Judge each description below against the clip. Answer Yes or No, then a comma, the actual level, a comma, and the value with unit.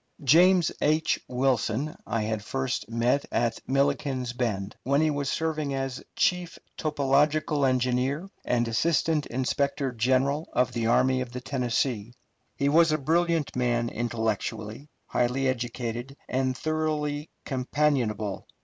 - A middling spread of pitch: Yes, average, 3.7 semitones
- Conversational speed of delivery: No, slow, 125 wpm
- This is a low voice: Yes, low, 130 Hz